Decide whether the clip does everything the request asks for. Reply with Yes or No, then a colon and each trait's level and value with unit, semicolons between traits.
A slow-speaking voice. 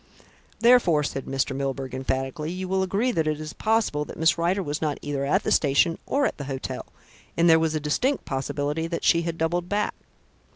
No: fast, 205 wpm